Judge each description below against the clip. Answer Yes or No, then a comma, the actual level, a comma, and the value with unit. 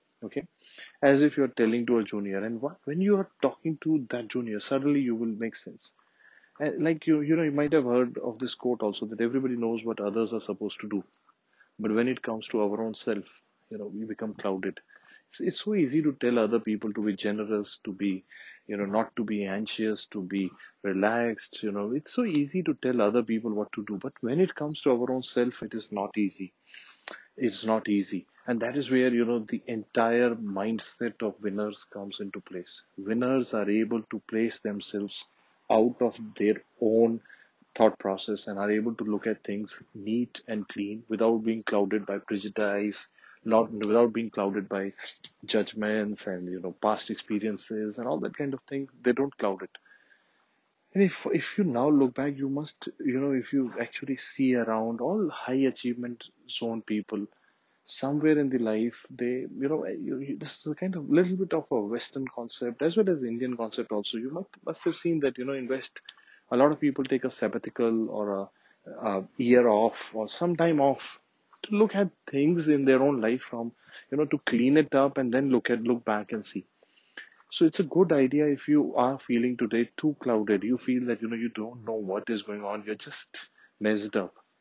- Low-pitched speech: Yes, low, 115 Hz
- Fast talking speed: Yes, fast, 210 wpm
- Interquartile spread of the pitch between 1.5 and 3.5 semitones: No, average, 4.3 semitones